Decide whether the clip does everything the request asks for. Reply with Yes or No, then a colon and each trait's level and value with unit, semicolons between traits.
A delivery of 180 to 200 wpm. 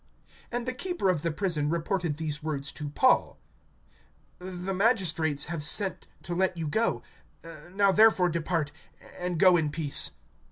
No: average, 150 wpm